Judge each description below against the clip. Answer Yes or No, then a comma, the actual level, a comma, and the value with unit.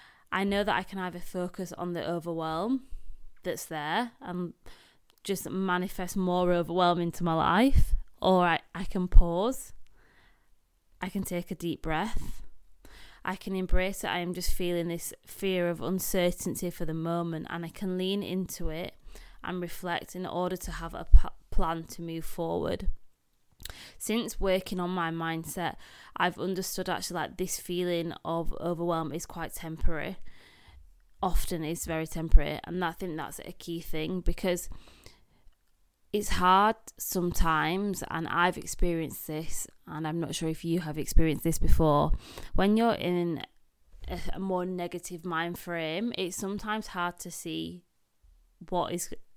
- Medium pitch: Yes, medium, 175 Hz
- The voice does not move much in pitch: Yes, narrow, 2.0 semitones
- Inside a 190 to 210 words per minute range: No, average, 150 wpm